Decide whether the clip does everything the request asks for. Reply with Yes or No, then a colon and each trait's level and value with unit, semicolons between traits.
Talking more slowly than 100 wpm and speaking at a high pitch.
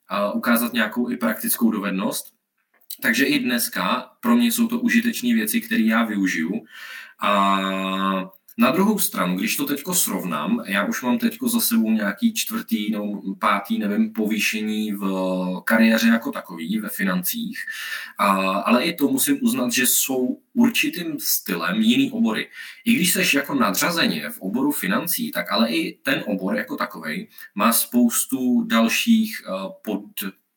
No: average, 145 wpm; high, 220 Hz